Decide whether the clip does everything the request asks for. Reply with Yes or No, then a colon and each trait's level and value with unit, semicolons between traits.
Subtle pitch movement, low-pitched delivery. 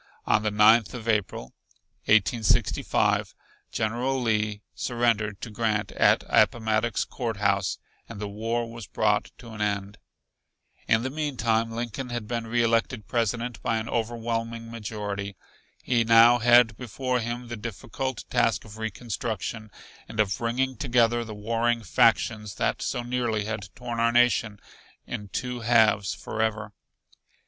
Yes: narrow, 1.9 semitones; low, 115 Hz